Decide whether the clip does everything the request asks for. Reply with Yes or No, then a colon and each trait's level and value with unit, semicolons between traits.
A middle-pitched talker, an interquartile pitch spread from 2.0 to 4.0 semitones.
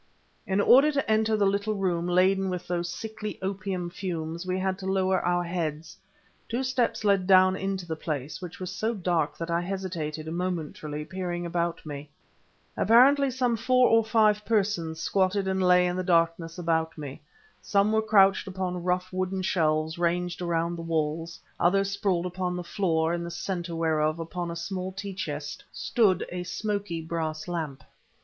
Yes: medium, 180 Hz; average, 2.8 semitones